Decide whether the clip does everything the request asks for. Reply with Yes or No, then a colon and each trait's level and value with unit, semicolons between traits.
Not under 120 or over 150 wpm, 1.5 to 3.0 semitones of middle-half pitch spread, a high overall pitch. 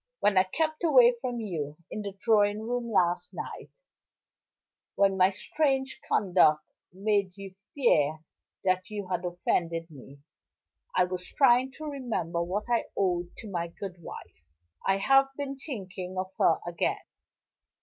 No: average, 145 wpm; average, 5.2 semitones; high, 195 Hz